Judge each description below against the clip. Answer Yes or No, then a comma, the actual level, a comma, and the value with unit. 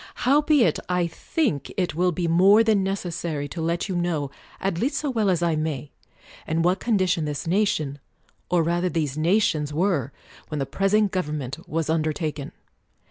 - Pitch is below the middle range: No, medium, 170 Hz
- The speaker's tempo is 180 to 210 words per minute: No, average, 170 wpm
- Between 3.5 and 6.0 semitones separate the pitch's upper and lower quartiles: Yes, average, 4.1 semitones